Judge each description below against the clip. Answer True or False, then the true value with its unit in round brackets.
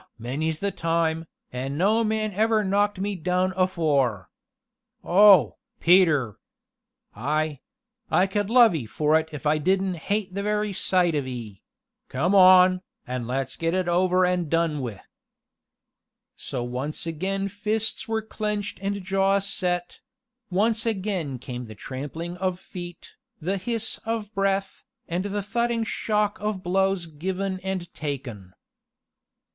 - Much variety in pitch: False (4.7 semitones)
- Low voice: False (185 Hz)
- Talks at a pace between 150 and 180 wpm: False (140 wpm)